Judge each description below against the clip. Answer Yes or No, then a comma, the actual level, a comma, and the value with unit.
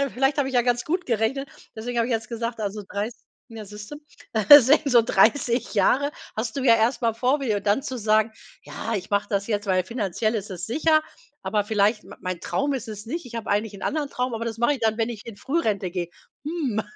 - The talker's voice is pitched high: Yes, high, 230 Hz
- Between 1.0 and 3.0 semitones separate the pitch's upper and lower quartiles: No, average, 3.5 semitones